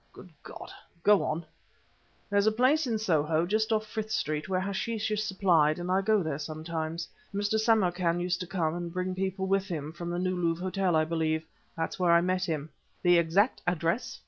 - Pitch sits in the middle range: Yes, medium, 180 Hz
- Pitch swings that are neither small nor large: Yes, average, 3.4 semitones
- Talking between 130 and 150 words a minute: No, average, 200 wpm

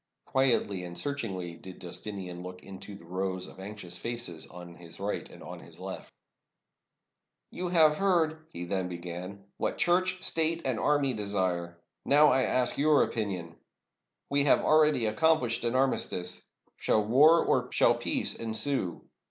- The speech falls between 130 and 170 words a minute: Yes, average, 150 wpm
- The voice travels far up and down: Yes, wide, 7.9 semitones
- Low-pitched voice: Yes, low, 110 Hz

